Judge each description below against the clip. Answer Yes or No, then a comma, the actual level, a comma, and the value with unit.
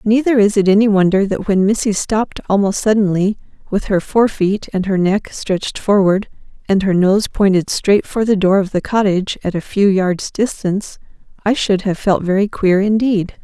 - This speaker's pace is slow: No, average, 190 wpm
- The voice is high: Yes, high, 200 Hz